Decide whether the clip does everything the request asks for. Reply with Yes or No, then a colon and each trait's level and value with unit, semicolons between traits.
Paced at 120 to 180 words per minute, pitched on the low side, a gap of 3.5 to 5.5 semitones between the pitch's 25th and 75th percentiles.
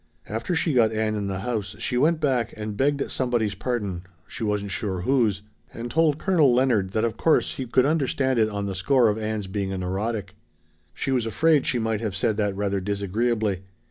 No: fast, 205 wpm; low, 110 Hz; average, 4.1 semitones